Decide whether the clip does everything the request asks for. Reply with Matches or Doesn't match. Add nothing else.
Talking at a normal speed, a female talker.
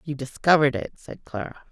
Matches